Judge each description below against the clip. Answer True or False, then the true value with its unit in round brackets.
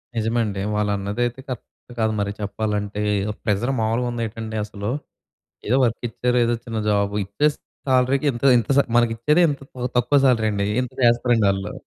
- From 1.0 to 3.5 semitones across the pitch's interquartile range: True (2.8 semitones)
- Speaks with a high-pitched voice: False (115 Hz)